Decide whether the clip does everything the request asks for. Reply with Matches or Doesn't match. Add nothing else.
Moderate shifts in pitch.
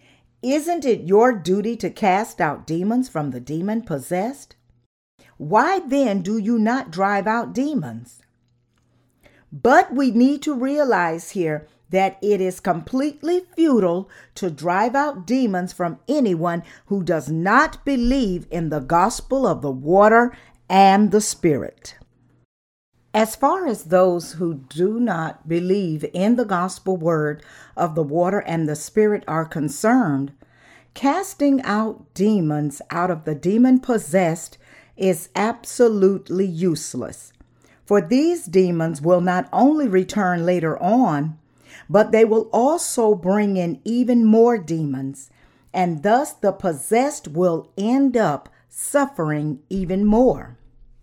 Doesn't match